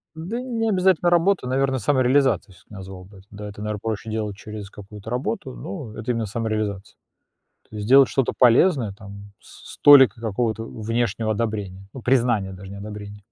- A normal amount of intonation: Yes, average, 4.2 semitones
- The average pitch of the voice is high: No, low, 110 Hz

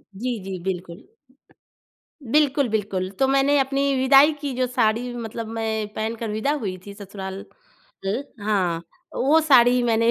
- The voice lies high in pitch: Yes, high, 230 Hz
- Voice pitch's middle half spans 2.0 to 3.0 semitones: No, average, 4.8 semitones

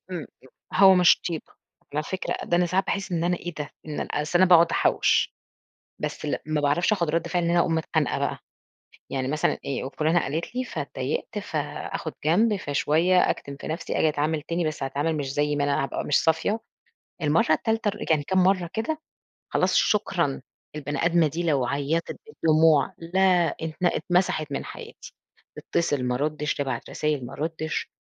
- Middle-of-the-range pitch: Yes, medium, 160 Hz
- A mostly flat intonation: No, average, 3.3 semitones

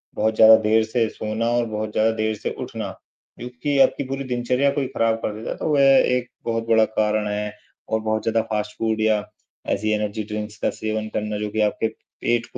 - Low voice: Yes, low, 110 Hz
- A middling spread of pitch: No, narrow, 1.7 semitones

